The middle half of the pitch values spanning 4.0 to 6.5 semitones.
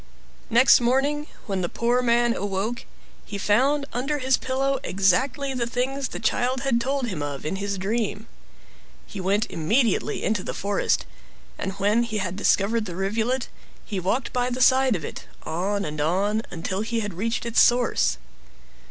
Yes: average, 4.3 semitones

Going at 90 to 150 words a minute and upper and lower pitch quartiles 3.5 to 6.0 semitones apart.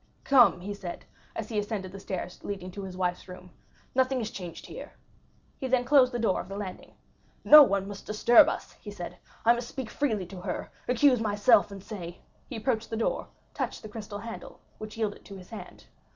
No: average, 200 wpm; average, 3.8 semitones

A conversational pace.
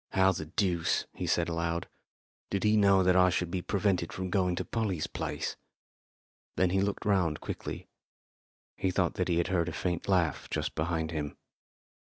Yes: average, 175 wpm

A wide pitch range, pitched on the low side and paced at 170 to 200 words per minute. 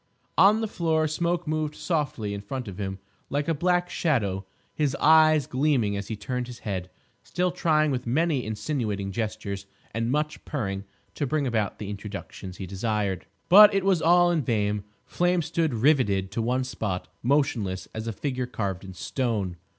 Yes: wide, 7.3 semitones; low, 125 Hz; average, 175 wpm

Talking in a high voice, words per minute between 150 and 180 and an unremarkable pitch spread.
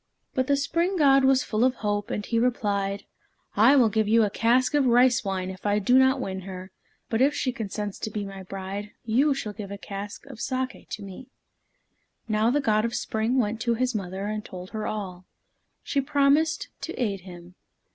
No: high, 220 Hz; average, 200 wpm; average, 4.3 semitones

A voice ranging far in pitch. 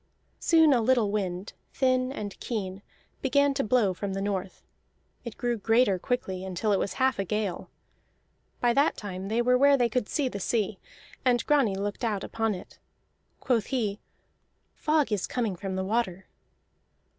No: average, 4.4 semitones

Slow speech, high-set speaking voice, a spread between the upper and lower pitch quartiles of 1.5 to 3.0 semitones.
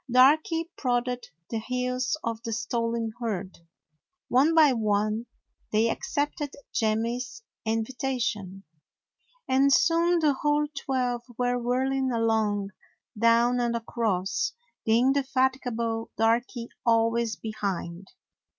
Yes: slow, 105 wpm; high, 240 Hz; average, 2.7 semitones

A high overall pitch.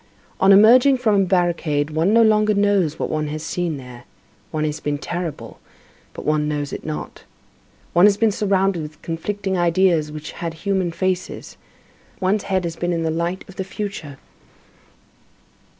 No: medium, 175 Hz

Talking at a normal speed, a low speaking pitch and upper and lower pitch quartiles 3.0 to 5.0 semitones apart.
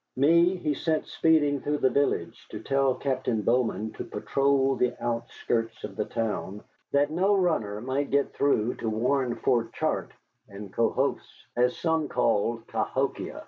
Yes: average, 150 wpm; low, 130 Hz; average, 3.9 semitones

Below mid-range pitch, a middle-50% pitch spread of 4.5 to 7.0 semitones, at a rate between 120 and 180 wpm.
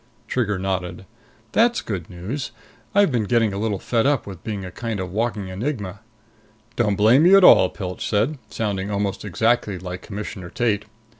No: low, 105 Hz; average, 3.9 semitones; average, 170 wpm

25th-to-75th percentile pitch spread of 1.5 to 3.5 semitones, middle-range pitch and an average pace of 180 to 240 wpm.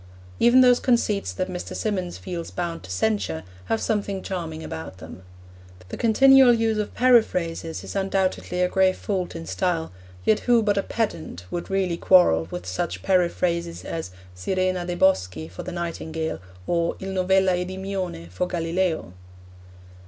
No: average, 3.0 semitones; medium, 180 Hz; average, 150 wpm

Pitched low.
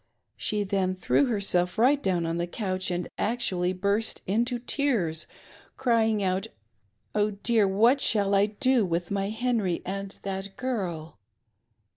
No: high, 200 Hz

